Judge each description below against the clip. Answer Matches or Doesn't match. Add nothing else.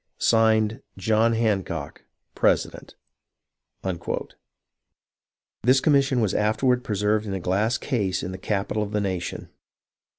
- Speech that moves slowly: Matches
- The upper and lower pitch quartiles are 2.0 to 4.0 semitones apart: Matches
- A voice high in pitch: Doesn't match